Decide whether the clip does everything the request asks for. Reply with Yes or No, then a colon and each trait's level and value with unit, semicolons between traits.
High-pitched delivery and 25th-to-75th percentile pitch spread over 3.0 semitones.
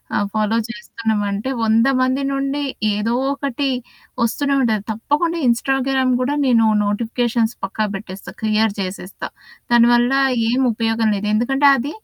Yes: high, 235 Hz; average, 3.6 semitones